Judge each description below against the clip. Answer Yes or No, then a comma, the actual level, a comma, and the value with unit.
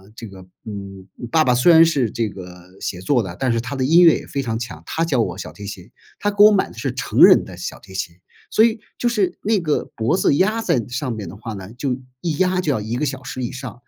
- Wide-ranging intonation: Yes, wide, 8.2 semitones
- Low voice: Yes, low, 125 Hz